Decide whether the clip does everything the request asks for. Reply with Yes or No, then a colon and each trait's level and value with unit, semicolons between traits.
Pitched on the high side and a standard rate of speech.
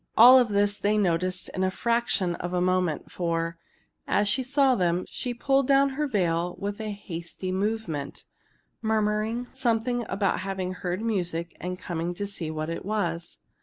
Yes: high, 195 Hz; average, 165 wpm